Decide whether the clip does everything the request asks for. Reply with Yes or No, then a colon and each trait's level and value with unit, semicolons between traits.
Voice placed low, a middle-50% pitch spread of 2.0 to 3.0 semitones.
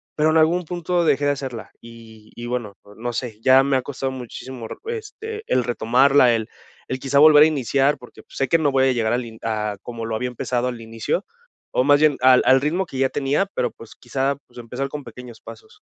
No: low, 130 Hz; average, 3.4 semitones